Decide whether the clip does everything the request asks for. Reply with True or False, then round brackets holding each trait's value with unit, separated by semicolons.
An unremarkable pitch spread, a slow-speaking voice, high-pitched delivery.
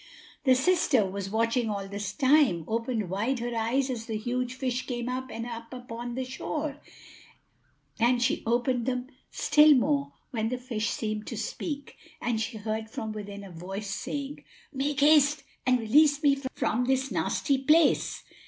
False (3.5 semitones; 170 wpm; 245 Hz)